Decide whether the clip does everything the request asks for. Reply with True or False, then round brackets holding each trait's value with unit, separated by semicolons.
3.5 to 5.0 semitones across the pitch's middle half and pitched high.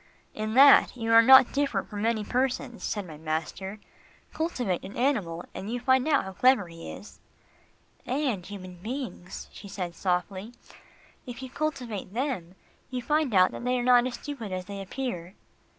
False (5.4 semitones; 225 Hz)